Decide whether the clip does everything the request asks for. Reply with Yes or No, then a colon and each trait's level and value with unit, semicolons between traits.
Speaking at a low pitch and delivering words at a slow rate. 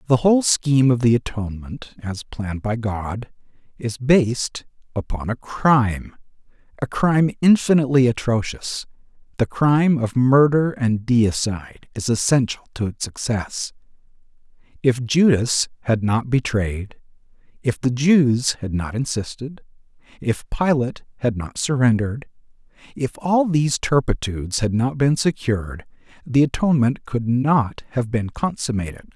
Yes: low, 125 Hz; slow, 125 wpm